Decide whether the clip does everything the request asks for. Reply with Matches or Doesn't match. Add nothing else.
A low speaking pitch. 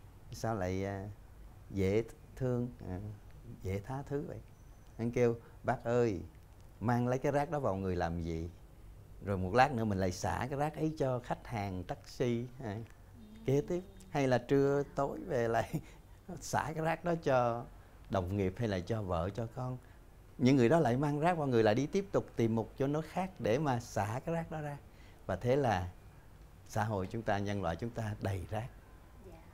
Matches